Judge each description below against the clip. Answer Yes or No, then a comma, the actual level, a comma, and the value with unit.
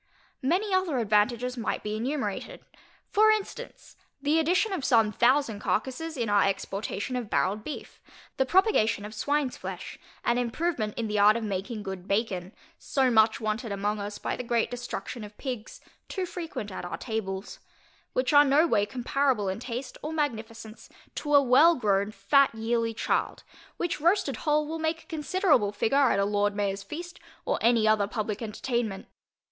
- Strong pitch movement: Yes, wide, 5.8 semitones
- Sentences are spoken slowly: No, average, 170 wpm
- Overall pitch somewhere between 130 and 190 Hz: No, high, 235 Hz